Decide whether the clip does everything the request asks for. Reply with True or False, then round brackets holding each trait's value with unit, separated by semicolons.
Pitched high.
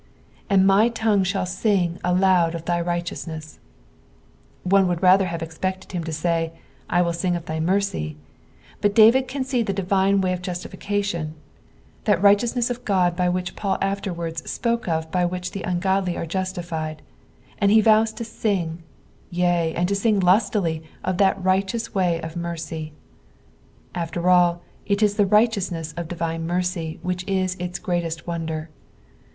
False (180 Hz)